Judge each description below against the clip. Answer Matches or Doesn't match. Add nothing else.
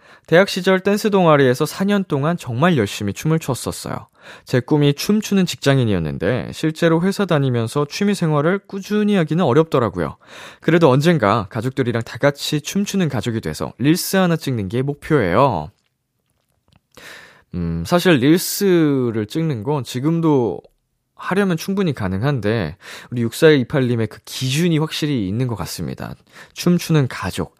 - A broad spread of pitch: Matches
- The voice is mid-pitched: Matches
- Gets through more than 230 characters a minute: Matches